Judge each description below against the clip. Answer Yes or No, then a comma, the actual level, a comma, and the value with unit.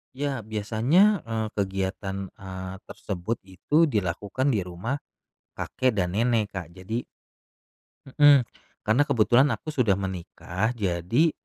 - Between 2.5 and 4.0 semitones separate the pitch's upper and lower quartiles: No, average, 4.9 semitones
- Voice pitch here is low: Yes, low, 110 Hz